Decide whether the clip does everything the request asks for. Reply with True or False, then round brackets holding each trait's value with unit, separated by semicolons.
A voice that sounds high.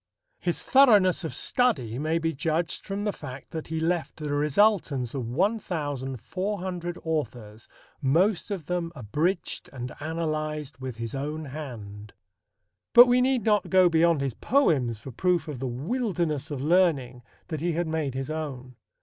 False (155 Hz)